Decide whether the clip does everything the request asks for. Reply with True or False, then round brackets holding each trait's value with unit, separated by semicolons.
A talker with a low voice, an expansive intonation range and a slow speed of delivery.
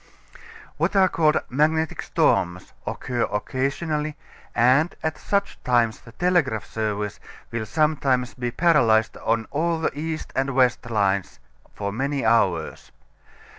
True (130 Hz; 5.8 semitones; 125 wpm)